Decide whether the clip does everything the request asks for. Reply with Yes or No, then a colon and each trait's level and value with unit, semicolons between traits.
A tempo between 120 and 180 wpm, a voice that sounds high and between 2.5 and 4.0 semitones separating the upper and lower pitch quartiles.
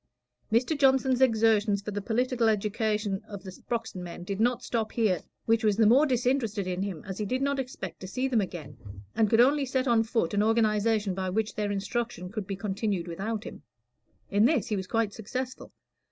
No: average, 200 wpm; high, 220 Hz; average, 3.4 semitones